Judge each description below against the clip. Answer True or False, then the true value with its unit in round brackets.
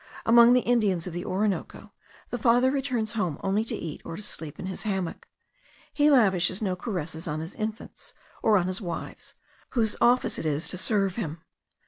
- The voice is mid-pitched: False (195 Hz)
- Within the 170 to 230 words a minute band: True (185 wpm)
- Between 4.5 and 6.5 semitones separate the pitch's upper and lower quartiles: True (4.9 semitones)